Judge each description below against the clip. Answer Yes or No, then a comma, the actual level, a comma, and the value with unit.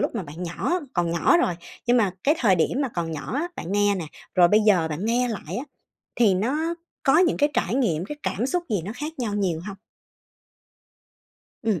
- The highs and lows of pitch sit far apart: Yes, wide, 7.0 semitones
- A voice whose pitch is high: Yes, high, 210 Hz